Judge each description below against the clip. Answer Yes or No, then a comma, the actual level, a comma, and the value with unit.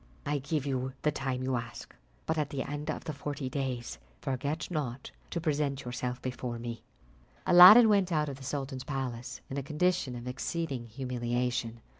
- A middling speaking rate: Yes, average, 175 wpm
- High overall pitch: No, low, 135 Hz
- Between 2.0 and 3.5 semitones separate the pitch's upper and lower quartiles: Yes, average, 3.1 semitones